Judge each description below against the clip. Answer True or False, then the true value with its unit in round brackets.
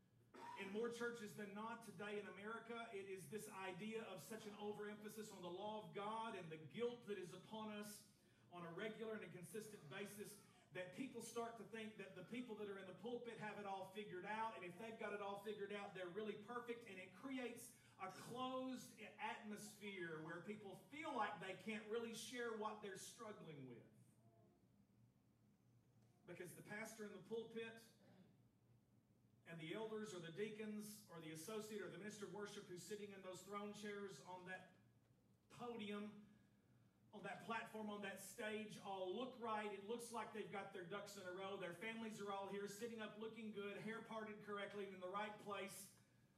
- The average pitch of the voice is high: True (210 Hz)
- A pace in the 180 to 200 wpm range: True (190 wpm)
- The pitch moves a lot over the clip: False (2.6 semitones)